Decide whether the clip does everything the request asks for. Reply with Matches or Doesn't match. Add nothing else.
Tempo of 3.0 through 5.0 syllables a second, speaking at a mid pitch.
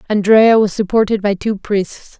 Doesn't match